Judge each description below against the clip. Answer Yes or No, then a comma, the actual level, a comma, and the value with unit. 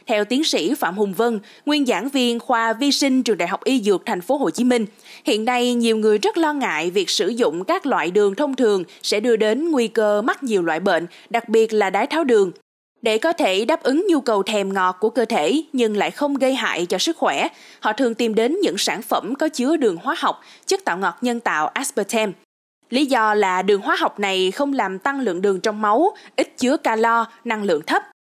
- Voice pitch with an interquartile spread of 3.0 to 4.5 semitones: No, average, 5.3 semitones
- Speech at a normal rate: Yes, average, 235 wpm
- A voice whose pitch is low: No, high, 235 Hz